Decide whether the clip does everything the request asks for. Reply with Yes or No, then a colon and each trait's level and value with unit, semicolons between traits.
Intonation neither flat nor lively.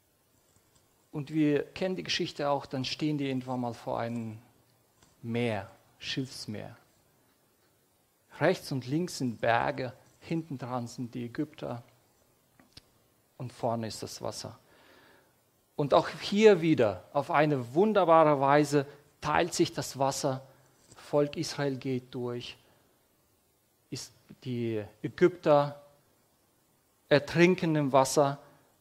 Yes: average, 3.5 semitones